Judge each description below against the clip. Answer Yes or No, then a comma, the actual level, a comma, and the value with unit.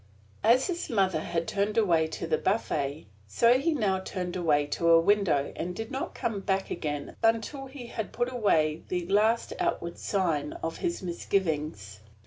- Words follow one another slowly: No, average, 165 wpm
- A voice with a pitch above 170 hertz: Yes, high, 190 Hz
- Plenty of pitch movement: Yes, wide, 5.7 semitones